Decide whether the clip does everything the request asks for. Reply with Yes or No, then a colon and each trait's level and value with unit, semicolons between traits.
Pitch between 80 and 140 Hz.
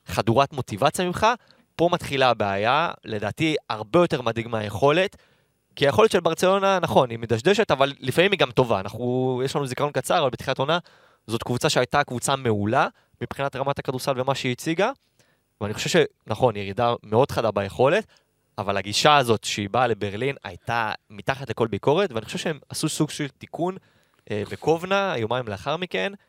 Yes: low, 135 Hz